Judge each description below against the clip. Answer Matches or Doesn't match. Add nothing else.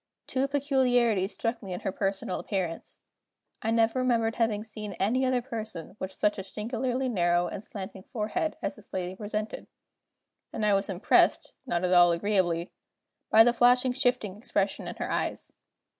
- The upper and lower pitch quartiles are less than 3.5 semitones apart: Doesn't match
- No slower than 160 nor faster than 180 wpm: Matches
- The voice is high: Matches